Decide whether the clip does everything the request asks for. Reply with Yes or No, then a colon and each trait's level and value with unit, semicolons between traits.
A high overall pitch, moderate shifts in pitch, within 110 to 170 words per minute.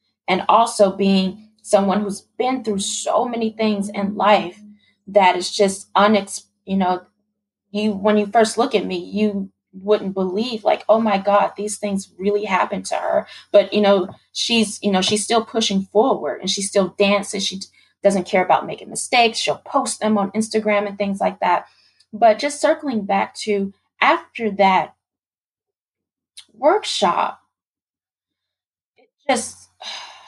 No: high, 205 Hz; narrow, 1.7 semitones; average, 155 wpm